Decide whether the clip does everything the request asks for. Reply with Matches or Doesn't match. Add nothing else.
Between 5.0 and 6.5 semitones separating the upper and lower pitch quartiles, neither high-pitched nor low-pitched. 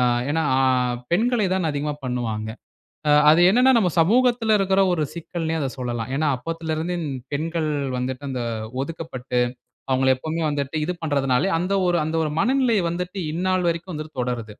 Matches